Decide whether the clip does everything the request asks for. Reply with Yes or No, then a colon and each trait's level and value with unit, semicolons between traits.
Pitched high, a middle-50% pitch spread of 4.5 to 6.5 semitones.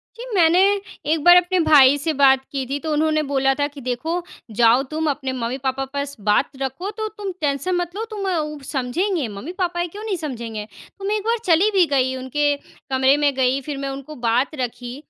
Yes: very high, 290 Hz; average, 5.0 semitones